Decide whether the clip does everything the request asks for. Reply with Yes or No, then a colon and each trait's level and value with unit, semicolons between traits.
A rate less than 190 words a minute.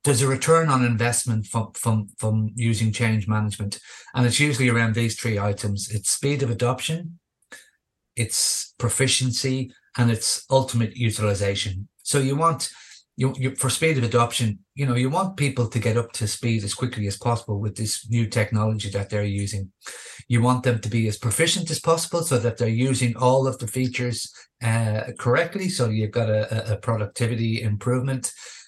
Yes: average, 175 wpm